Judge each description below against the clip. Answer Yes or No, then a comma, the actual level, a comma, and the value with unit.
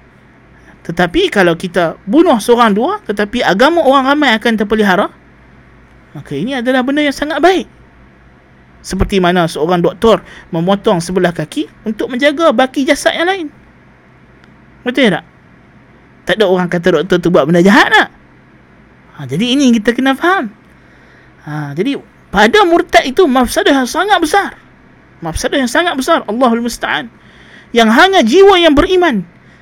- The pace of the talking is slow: No, average, 140 wpm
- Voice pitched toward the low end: No, high, 235 Hz